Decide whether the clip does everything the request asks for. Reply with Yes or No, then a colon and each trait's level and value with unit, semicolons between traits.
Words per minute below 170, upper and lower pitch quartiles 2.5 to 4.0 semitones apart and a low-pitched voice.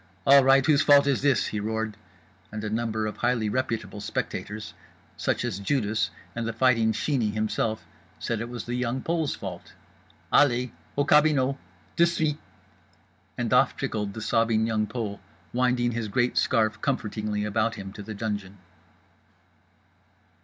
Yes: average, 155 wpm; average, 3.3 semitones; low, 115 Hz